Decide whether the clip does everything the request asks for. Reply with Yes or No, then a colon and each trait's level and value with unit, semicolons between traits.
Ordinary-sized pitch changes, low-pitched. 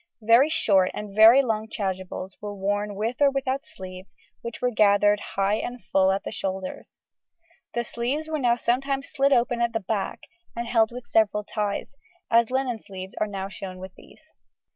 No: average, 3.9 semitones; high, 220 Hz